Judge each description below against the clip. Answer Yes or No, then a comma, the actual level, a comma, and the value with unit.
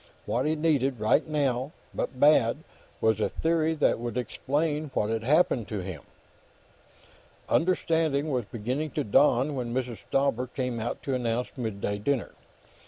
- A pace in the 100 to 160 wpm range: Yes, average, 150 wpm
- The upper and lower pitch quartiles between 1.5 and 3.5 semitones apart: No, average, 4.6 semitones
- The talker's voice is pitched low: Yes, low, 130 Hz